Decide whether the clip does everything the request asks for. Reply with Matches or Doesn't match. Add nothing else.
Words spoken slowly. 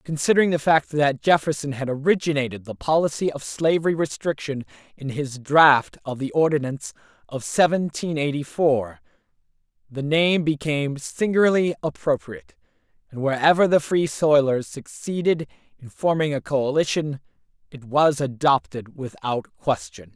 Matches